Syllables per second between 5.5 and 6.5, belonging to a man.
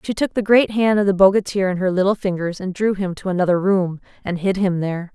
No: 6.0 syllables/s; female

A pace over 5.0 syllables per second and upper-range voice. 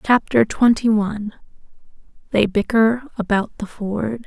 No: 4.2 syllables/s; high, 220 Hz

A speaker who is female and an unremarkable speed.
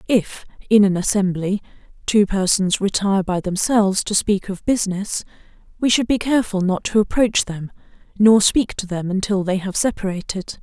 Yes: female; average, 165 wpm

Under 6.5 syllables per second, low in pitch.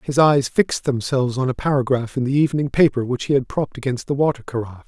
No: 6.8 syllables/s; low, 130 Hz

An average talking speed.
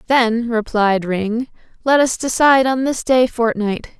Yes: average, 150 wpm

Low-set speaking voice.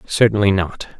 Yes: low, 100 Hz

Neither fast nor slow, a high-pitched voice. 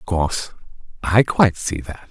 No: average, 170 wpm; very low, 90 Hz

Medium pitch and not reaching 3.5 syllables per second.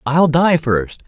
Yes: medium, 150 Hz; 3.2 syllables/s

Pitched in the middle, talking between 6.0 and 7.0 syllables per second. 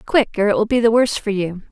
No: high, 215 Hz; 6.5 syllables/s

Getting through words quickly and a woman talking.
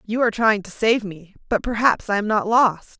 Yes: fast, 240 wpm; female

